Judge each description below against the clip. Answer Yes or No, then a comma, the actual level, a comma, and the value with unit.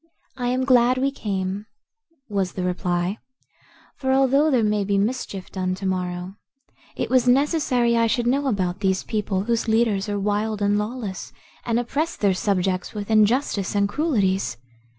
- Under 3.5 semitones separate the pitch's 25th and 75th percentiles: No, average, 4.3 semitones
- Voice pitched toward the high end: Yes, high, 210 Hz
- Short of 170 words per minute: Yes, average, 160 wpm